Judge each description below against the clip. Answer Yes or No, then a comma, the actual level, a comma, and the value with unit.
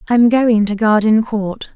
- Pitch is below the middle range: No, high, 220 Hz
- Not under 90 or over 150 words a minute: Yes, slow, 135 wpm